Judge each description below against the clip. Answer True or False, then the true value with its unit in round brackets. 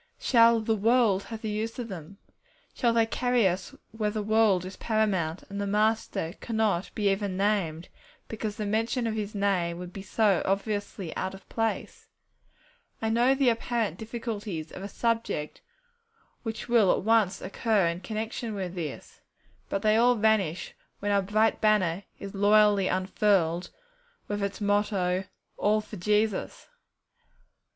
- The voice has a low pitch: False (210 Hz)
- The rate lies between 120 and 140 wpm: False (155 wpm)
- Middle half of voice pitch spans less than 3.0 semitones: True (2.6 semitones)